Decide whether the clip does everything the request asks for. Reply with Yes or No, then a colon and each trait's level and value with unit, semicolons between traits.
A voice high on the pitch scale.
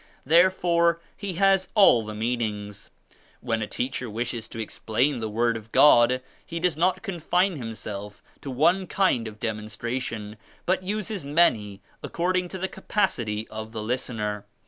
No: low, 125 Hz